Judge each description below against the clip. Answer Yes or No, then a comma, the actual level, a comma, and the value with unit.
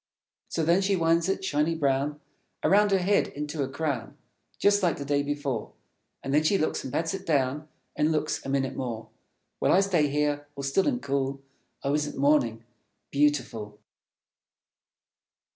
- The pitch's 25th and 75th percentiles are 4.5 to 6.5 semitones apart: No, average, 3.3 semitones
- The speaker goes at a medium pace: Yes, average, 165 wpm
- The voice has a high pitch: No, medium, 150 Hz